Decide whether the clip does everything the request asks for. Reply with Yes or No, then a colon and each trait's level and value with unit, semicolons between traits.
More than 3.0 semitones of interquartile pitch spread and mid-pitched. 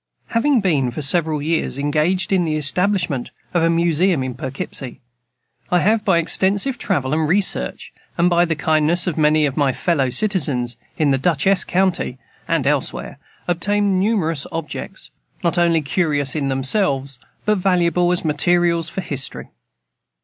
Yes: average, 4.1 semitones; medium, 165 Hz